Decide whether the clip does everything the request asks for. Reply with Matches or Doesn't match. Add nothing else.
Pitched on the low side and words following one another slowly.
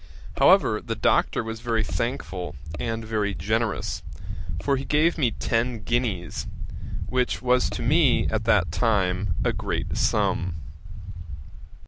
Matches